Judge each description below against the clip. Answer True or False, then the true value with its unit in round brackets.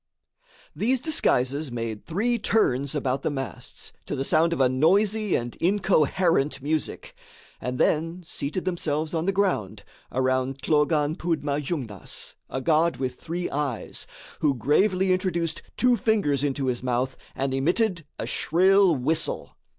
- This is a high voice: False (155 Hz)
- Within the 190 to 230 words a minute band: False (140 wpm)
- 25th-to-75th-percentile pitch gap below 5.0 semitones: False (5.5 semitones)